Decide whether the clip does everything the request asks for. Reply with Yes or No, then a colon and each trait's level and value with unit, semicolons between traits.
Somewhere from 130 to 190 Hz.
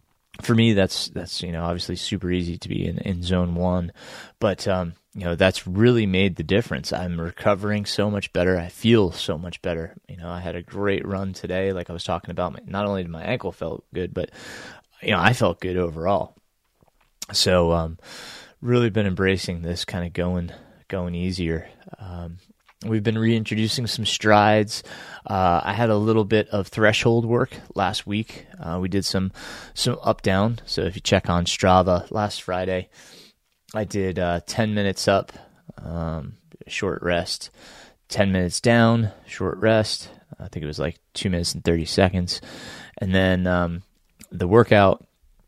No: very low, 95 Hz